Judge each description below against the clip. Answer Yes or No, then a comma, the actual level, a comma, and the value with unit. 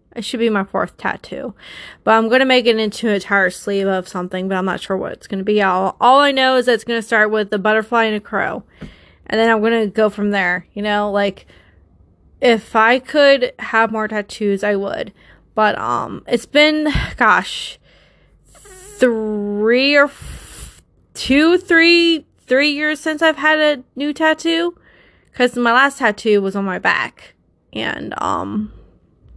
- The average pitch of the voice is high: Yes, high, 225 Hz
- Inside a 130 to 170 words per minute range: No, average, 185 wpm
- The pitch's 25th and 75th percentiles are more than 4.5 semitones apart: Yes, average, 4.9 semitones